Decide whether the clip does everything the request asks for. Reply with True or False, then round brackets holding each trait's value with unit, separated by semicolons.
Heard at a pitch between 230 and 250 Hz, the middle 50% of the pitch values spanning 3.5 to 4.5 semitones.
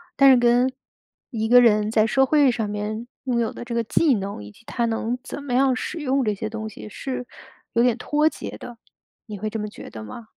False (235 Hz; 3.1 semitones)